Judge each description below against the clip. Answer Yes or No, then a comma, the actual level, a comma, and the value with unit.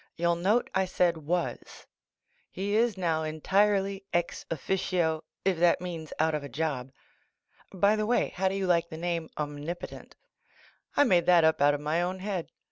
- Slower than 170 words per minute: No, average, 175 wpm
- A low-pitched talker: No, medium, 175 Hz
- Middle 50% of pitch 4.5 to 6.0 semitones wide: No, average, 3.2 semitones